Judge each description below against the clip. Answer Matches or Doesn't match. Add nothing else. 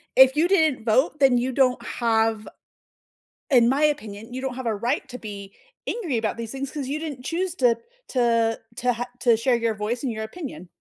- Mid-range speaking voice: Doesn't match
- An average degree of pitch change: Matches